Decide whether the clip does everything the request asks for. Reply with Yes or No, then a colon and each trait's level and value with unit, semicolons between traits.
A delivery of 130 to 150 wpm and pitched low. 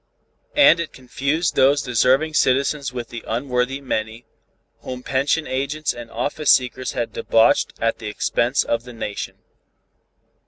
Yes: slow, 135 wpm; low, 130 Hz